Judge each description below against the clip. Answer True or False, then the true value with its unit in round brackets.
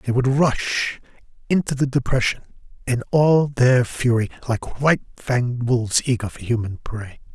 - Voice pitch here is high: False (125 Hz)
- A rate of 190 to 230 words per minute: False (145 wpm)